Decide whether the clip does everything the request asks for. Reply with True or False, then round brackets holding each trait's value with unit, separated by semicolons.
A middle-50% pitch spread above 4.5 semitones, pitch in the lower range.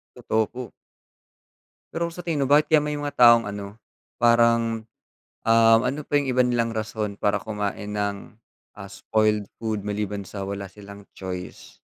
False (3.3 semitones; 110 Hz)